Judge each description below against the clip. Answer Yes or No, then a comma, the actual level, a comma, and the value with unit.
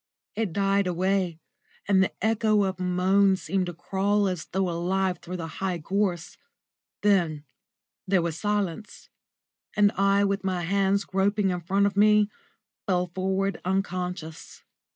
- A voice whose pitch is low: No, high, 190 Hz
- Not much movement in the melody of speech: Yes, narrow, 1.9 semitones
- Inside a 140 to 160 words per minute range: Yes, average, 145 wpm